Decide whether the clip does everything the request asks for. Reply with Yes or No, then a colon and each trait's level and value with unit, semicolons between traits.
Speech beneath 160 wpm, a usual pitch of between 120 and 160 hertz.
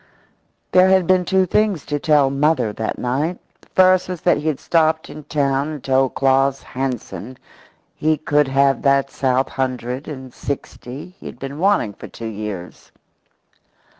No: average, 165 wpm; medium, 140 Hz